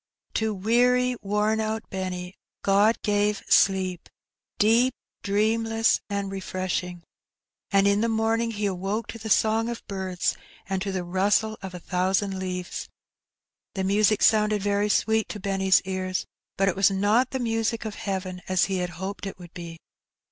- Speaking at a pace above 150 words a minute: Yes, average, 160 wpm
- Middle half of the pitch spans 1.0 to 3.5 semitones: Yes, average, 2.7 semitones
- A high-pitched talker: Yes, high, 200 Hz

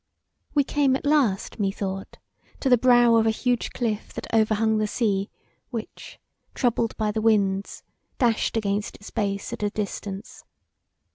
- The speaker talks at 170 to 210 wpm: No, average, 155 wpm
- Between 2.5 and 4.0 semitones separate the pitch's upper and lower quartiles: Yes, average, 3.0 semitones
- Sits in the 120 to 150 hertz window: No, high, 220 Hz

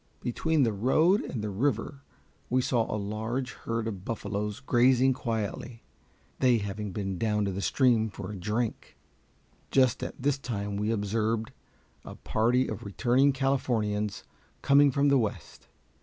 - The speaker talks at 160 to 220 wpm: No, average, 150 wpm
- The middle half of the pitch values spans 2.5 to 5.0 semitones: Yes, average, 3.8 semitones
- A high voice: No, low, 115 Hz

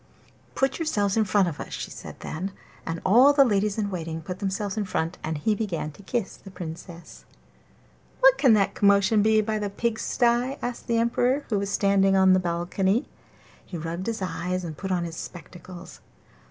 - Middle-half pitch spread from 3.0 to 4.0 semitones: Yes, average, 3.7 semitones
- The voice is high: Yes, high, 195 Hz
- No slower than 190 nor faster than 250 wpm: Yes, average, 195 wpm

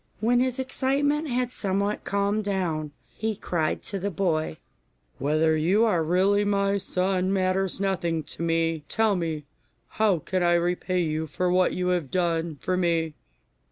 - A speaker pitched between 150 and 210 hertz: Yes, medium, 185 Hz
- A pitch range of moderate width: Yes, average, 3.5 semitones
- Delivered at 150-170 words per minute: Yes, average, 155 wpm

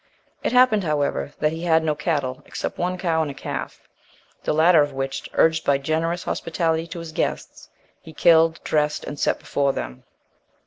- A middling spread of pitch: No, narrow, 2.3 semitones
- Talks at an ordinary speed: Yes, average, 180 wpm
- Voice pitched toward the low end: No, medium, 160 Hz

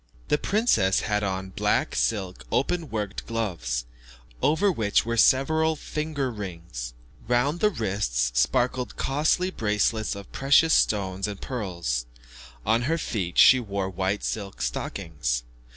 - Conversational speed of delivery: No, slow, 130 wpm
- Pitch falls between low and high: No, low, 105 Hz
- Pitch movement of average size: No, wide, 6.3 semitones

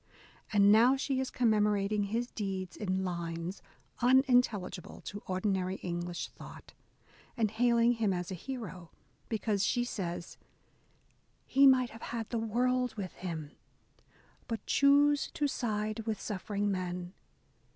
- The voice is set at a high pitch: Yes, high, 210 Hz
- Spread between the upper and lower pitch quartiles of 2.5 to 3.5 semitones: No, average, 4.5 semitones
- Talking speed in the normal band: No, slow, 130 wpm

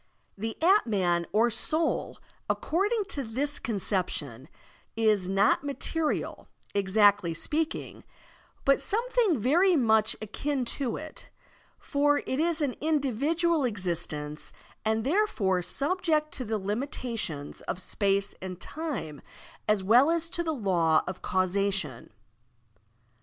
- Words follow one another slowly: Yes, slow, 115 wpm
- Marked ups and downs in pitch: Yes, wide, 8.0 semitones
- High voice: Yes, high, 230 Hz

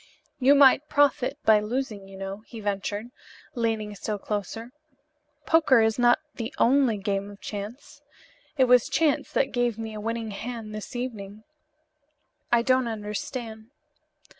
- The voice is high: Yes, high, 225 Hz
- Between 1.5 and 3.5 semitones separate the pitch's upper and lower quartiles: Yes, average, 3.2 semitones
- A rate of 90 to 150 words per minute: Yes, average, 140 wpm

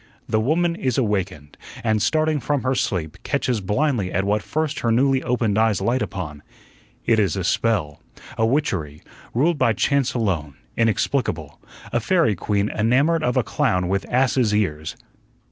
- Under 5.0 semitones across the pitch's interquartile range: No, wide, 5.5 semitones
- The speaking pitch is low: Yes, low, 115 Hz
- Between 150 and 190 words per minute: Yes, average, 160 wpm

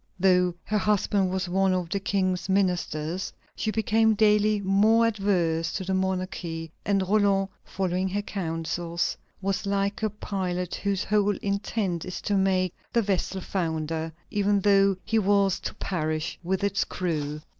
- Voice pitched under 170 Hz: No, high, 190 Hz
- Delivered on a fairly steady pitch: Yes, narrow, 2.1 semitones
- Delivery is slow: No, average, 150 wpm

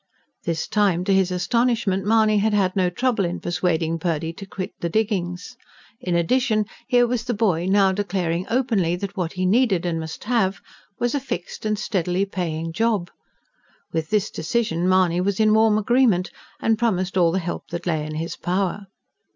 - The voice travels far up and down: No, average, 3.8 semitones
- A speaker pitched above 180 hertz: Yes, high, 190 Hz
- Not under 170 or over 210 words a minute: Yes, average, 180 wpm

